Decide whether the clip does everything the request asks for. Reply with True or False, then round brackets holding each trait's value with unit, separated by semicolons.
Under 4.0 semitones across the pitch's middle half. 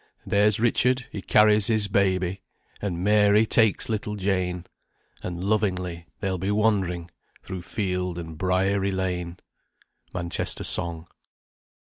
True (2.7 semitones)